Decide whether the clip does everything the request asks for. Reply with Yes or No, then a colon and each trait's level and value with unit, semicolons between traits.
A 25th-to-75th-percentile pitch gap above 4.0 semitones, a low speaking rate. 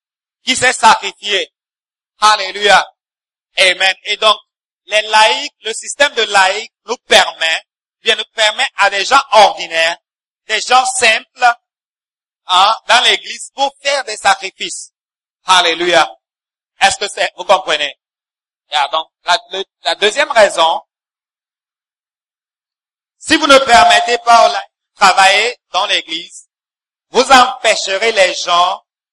Yes: wide, 5.4 semitones; slow, 120 wpm